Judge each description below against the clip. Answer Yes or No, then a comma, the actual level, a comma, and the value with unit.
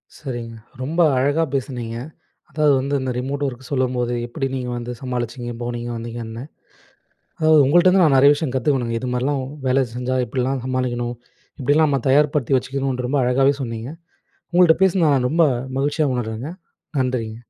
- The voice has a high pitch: No, low, 130 Hz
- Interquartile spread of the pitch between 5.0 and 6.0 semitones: No, average, 2.7 semitones